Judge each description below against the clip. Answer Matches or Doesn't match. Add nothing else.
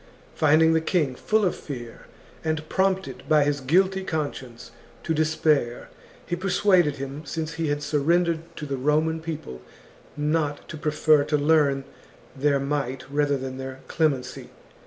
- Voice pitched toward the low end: Doesn't match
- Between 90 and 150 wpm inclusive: Matches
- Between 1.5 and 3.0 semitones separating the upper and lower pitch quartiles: Matches